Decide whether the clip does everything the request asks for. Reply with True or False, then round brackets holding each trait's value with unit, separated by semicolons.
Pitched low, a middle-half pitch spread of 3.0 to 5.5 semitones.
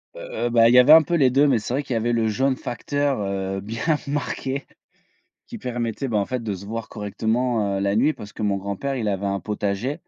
True (115 Hz; 4.8 semitones)